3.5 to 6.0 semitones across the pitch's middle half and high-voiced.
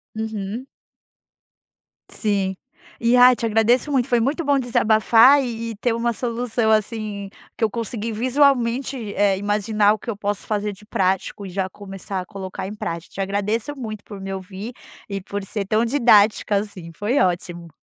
No: average, 3.0 semitones; high, 215 Hz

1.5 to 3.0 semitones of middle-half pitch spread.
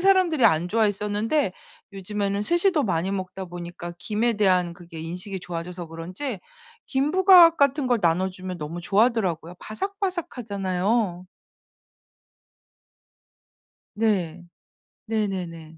No: average, 5.2 semitones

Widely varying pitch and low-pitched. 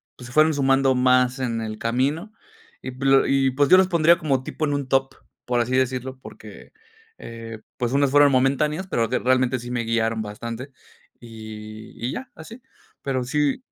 No: average, 3.0 semitones; low, 130 Hz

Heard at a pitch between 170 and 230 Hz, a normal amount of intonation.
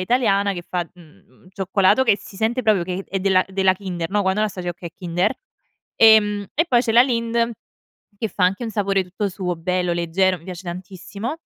Yes: high, 190 Hz; average, 3.0 semitones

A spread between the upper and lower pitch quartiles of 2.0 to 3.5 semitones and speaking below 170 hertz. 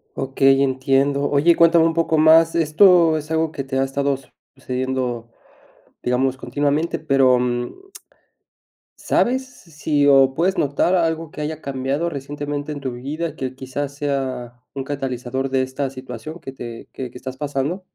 Yes: average, 3.2 semitones; medium, 140 Hz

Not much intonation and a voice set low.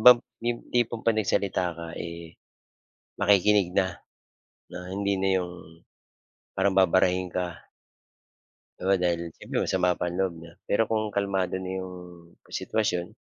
Yes: narrow, 2.2 semitones; very low, 95 Hz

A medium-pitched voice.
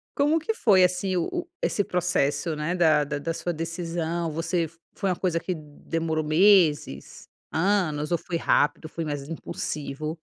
Yes: medium, 165 Hz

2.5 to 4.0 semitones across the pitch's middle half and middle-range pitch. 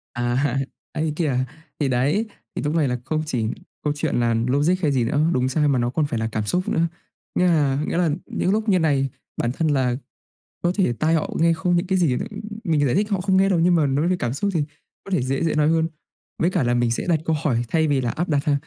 No: average, 4.7 semitones; medium, 150 Hz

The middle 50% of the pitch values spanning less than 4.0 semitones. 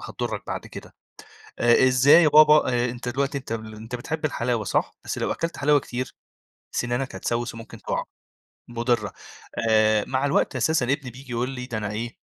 Yes: average, 2.7 semitones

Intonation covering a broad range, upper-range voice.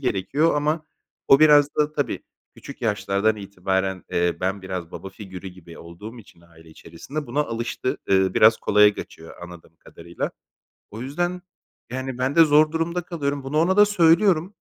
No: wide, 8.3 semitones; low, 115 Hz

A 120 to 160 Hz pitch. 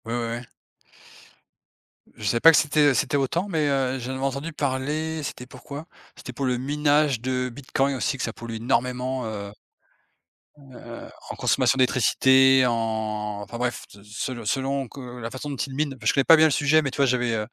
Yes: low, 130 Hz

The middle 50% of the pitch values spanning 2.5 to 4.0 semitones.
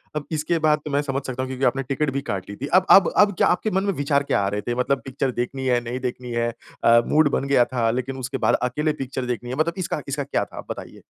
Yes: average, 3.0 semitones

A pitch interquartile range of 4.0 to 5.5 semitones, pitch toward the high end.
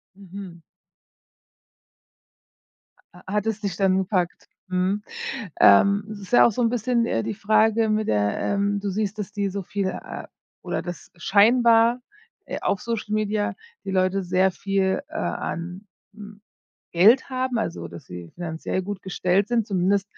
No: narrow, 2.6 semitones; high, 200 Hz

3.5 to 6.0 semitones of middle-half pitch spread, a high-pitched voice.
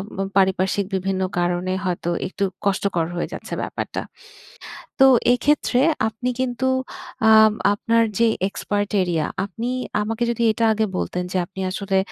Yes: average, 3.8 semitones; high, 200 Hz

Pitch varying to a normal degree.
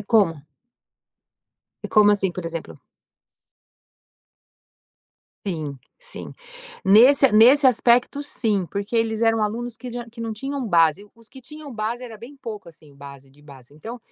No: wide, 5.8 semitones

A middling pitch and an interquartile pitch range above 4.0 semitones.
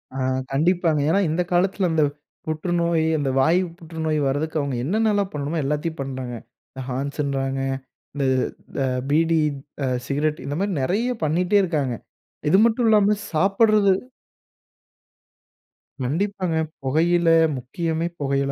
Yes: medium, 160 Hz; average, 4.4 semitones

